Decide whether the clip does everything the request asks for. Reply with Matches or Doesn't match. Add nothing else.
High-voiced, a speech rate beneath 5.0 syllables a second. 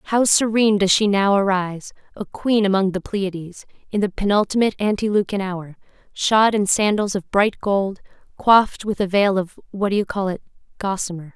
Doesn't match